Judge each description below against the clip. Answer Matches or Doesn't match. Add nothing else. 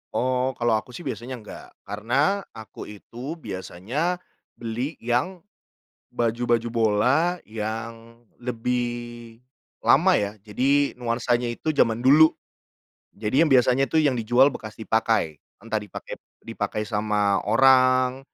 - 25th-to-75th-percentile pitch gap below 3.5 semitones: Matches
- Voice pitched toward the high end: Doesn't match